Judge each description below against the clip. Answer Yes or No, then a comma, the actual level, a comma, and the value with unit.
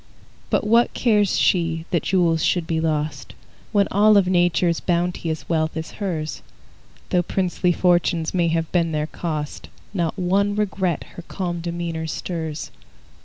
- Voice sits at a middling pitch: Yes, medium, 175 Hz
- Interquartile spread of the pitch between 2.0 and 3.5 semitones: Yes, narrow, 2.4 semitones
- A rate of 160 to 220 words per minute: No, average, 145 wpm